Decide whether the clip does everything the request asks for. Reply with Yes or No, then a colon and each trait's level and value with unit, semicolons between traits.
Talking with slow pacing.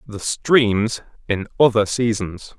Yes: slow, 115 wpm